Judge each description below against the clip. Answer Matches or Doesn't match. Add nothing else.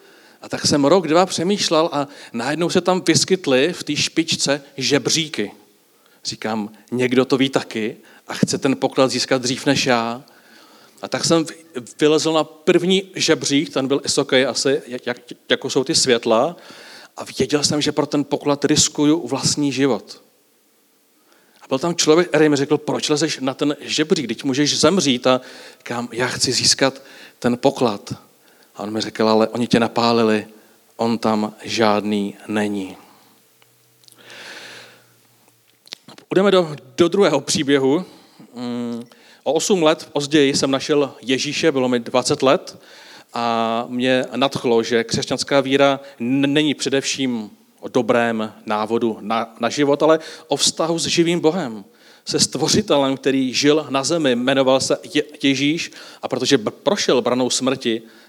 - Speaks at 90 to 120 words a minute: Doesn't match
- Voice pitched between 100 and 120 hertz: Doesn't match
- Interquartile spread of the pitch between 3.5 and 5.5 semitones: Matches